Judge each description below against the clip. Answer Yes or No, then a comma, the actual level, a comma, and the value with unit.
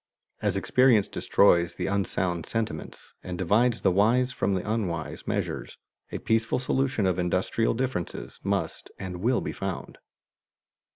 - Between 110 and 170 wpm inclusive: Yes, slow, 135 wpm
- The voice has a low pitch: Yes, low, 100 Hz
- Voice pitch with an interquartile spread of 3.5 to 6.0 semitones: Yes, average, 4.4 semitones